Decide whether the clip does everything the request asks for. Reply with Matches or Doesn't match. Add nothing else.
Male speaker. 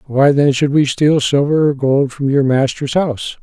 Matches